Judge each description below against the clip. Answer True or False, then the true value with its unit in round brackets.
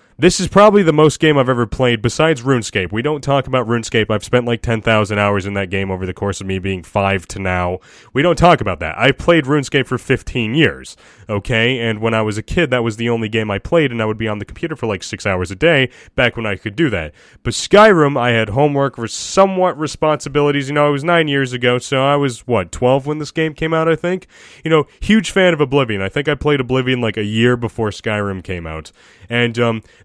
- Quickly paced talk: True (250 wpm)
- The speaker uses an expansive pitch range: True (5.7 semitones)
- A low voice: True (125 Hz)